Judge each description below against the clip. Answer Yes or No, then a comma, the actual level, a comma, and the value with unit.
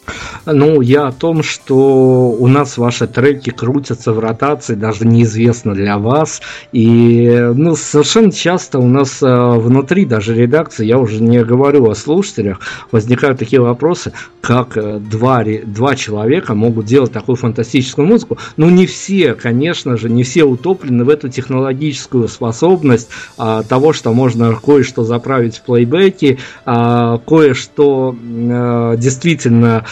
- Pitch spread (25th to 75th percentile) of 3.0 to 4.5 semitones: Yes, average, 3.7 semitones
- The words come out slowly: No, average, 130 wpm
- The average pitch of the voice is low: Yes, low, 125 Hz